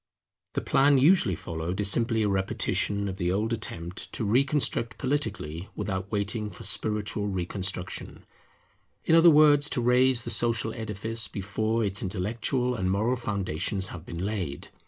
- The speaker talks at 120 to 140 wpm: No, average, 150 wpm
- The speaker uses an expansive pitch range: No, average, 3.8 semitones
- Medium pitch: No, low, 105 Hz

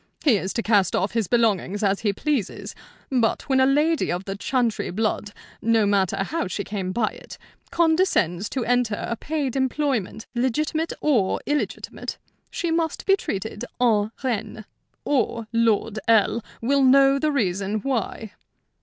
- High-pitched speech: Yes, high, 230 Hz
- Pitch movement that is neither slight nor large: Yes, average, 4.9 semitones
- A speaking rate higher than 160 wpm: No, average, 155 wpm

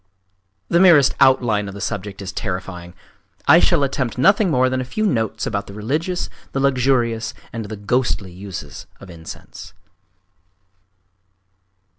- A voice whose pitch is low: Yes, low, 115 Hz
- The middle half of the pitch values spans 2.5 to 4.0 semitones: No, average, 5.3 semitones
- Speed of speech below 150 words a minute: Yes, average, 140 wpm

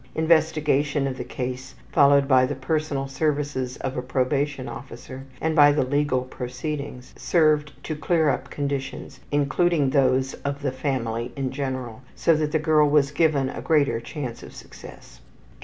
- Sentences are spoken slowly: No, average, 155 wpm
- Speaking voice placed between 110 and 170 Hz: Yes, medium, 140 Hz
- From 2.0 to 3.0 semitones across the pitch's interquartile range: Yes, narrow, 2.5 semitones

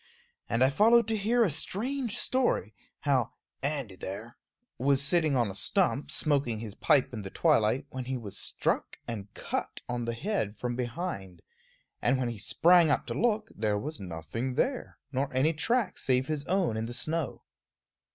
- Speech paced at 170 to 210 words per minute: Yes, average, 175 wpm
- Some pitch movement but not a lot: No, wide, 7.1 semitones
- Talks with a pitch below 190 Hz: Yes, low, 135 Hz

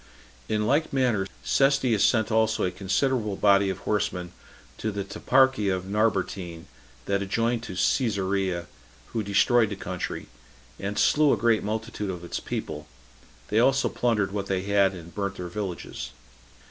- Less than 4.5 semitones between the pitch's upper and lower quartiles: Yes, average, 3.0 semitones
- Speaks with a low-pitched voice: Yes, low, 100 Hz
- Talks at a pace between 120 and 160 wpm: Yes, average, 150 wpm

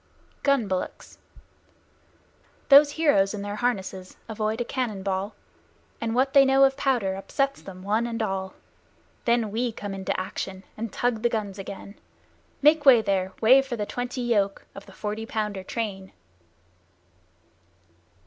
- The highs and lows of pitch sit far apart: No, average, 4.0 semitones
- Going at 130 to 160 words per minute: Yes, average, 150 wpm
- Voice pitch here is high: Yes, high, 220 Hz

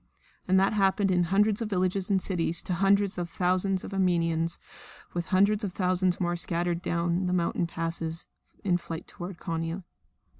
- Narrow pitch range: Yes, narrow, 2.2 semitones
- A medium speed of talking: Yes, average, 165 wpm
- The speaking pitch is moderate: Yes, medium, 180 Hz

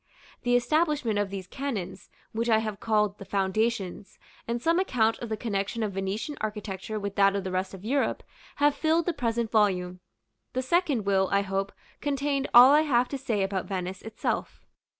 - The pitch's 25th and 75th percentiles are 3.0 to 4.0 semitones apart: No, average, 4.7 semitones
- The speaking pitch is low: No, high, 220 Hz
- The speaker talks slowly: No, average, 185 wpm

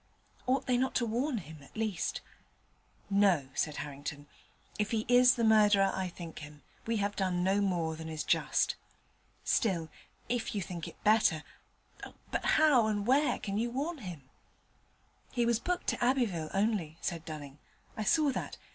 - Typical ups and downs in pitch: No, wide, 6.5 semitones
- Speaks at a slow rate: No, average, 165 wpm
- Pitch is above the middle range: Yes, high, 205 Hz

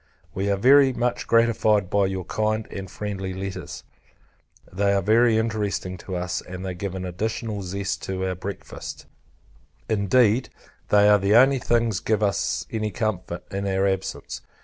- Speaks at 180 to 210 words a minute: No, average, 160 wpm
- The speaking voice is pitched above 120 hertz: No, low, 100 Hz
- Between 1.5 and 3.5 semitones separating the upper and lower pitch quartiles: Yes, narrow, 2.6 semitones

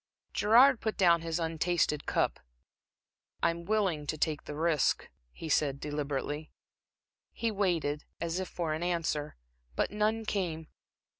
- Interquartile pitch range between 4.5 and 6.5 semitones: No, average, 4.1 semitones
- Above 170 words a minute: No, slow, 135 wpm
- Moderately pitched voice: Yes, medium, 165 Hz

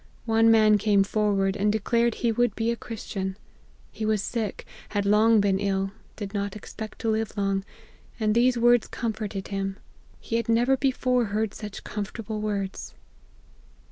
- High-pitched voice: Yes, high, 215 Hz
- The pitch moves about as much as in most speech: No, narrow, 2.2 semitones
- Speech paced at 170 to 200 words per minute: No, average, 160 wpm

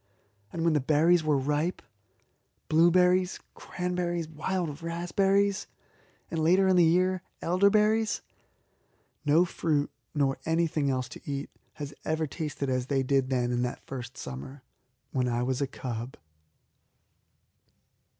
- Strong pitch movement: No, average, 4.8 semitones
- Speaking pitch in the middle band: Yes, medium, 155 Hz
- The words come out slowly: Yes, slow, 130 wpm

